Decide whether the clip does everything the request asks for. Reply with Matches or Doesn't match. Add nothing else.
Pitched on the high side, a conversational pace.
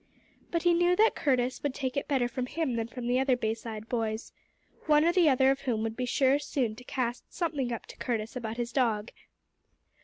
Doesn't match